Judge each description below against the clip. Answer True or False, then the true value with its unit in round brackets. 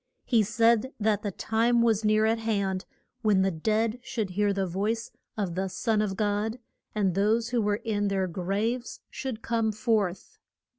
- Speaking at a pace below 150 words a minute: False (175 wpm)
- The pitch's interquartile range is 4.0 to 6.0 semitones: False (2.4 semitones)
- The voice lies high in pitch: True (215 Hz)